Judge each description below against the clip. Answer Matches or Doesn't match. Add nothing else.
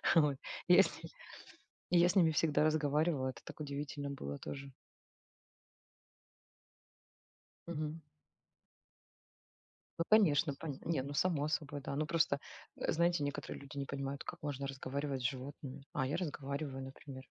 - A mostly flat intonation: Matches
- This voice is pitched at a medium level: Matches